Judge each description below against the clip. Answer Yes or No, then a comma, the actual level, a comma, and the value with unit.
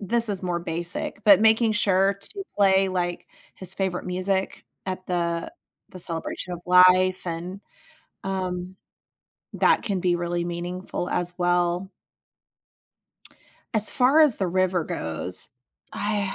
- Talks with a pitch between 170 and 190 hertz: Yes, medium, 185 Hz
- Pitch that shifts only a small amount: Yes, narrow, 1.9 semitones